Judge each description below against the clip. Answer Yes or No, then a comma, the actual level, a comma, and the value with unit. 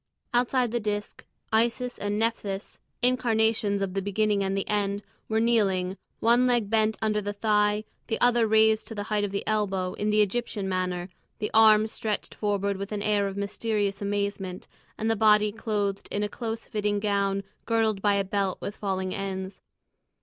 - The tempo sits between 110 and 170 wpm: No, average, 180 wpm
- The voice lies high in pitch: Yes, high, 210 Hz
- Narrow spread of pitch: Yes, narrow, 1.8 semitones